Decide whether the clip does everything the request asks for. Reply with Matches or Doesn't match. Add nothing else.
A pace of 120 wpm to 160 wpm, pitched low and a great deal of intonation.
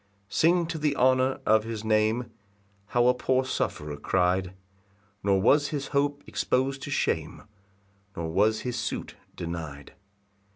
Matches